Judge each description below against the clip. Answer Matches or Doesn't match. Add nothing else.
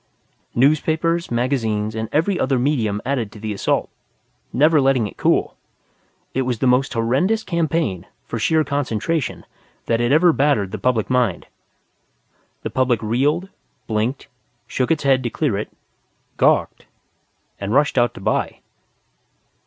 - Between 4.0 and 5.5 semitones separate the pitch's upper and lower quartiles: Matches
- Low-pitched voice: Matches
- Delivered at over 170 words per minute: Doesn't match